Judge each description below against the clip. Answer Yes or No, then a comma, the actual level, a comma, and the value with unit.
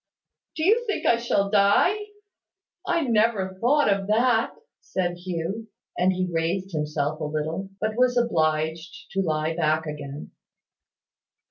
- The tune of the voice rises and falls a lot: Yes, wide, 6.0 semitones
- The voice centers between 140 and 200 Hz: Yes, high, 190 Hz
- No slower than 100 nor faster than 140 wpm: Yes, slow, 135 wpm